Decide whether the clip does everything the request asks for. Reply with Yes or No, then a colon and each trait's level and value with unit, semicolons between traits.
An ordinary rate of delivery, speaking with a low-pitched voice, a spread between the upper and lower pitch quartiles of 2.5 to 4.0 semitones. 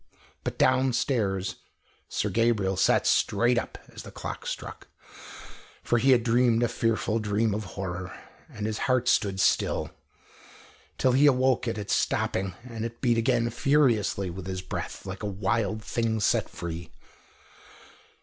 Yes: average, 150 wpm; low, 115 Hz; average, 3.7 semitones